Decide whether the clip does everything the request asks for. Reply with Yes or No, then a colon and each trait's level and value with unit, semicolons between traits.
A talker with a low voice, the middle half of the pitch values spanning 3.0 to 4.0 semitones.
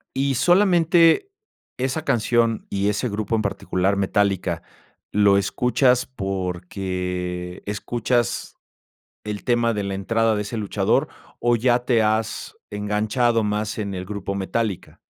Yes: low, 105 Hz; average, 3.4 semitones